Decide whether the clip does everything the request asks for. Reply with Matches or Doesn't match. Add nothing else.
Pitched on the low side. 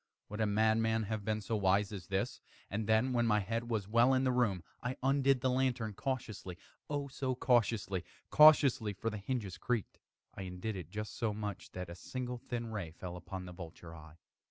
Matches